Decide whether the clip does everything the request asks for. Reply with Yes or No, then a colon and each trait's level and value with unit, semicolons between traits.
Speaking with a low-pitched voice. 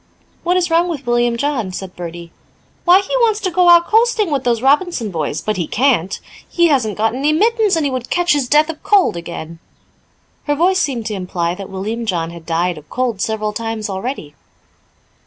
No: high, 240 Hz